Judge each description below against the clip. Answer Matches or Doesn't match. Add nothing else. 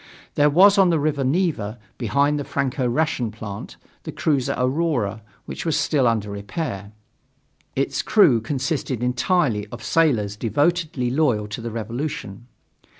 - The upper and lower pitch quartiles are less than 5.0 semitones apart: Doesn't match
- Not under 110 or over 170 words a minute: Matches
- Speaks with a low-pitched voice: Matches